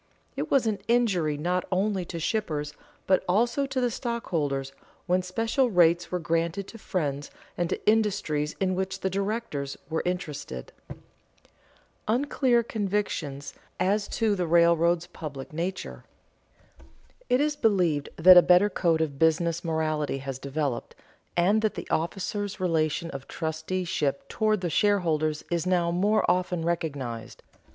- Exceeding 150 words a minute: No, average, 140 wpm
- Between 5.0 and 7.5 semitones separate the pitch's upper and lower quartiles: No, average, 4.6 semitones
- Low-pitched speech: No, medium, 175 Hz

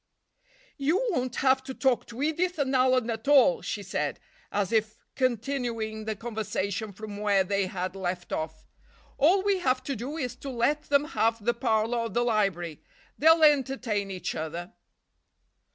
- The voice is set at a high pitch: Yes, high, 235 Hz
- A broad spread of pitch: No, average, 4.8 semitones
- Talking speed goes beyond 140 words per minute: Yes, average, 165 wpm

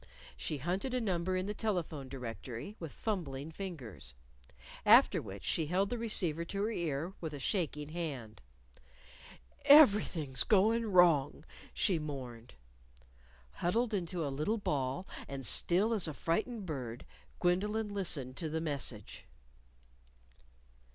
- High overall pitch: No, medium, 170 Hz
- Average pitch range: No, wide, 6.4 semitones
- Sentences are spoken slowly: Yes, slow, 130 wpm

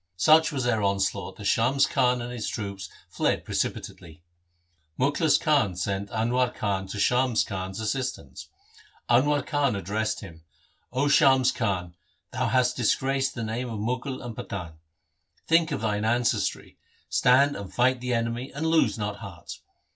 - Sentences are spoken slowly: No, average, 155 wpm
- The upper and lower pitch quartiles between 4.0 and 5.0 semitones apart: Yes, average, 4.5 semitones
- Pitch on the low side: Yes, low, 120 Hz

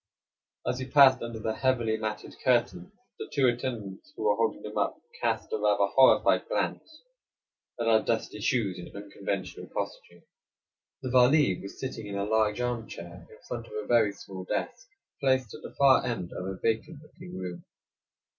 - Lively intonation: No, average, 4.3 semitones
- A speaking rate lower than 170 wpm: No, average, 175 wpm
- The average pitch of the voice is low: Yes, low, 115 Hz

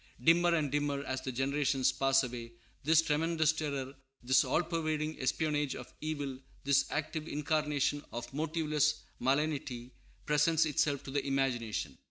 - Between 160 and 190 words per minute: No, average, 140 wpm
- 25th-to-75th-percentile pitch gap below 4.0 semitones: Yes, narrow, 2.6 semitones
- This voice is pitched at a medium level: Yes, medium, 145 Hz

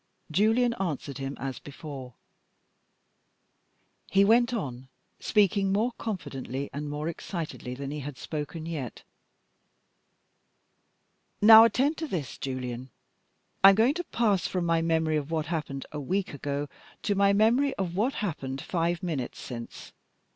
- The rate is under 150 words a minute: Yes, average, 140 wpm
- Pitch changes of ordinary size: No, wide, 6.4 semitones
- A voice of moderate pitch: Yes, medium, 165 Hz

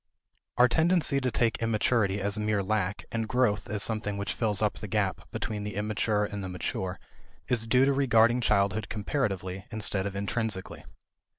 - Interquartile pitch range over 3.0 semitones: No, narrow, 2.6 semitones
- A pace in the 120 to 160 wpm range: No, average, 170 wpm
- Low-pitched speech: Yes, low, 105 Hz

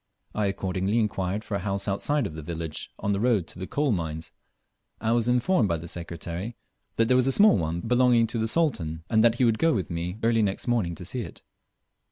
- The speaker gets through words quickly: Yes, fast, 230 wpm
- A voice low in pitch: Yes, low, 105 Hz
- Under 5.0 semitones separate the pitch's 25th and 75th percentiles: No, average, 5.3 semitones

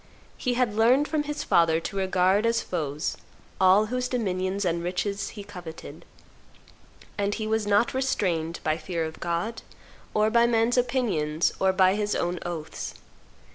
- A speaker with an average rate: Yes, average, 155 wpm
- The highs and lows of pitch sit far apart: No, average, 4.8 semitones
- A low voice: No, high, 200 Hz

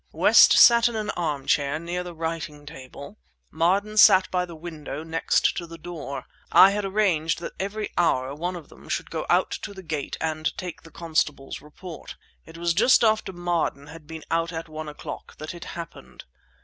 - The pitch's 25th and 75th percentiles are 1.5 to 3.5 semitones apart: Yes, average, 2.9 semitones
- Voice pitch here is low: No, medium, 165 Hz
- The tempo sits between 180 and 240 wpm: Yes, average, 190 wpm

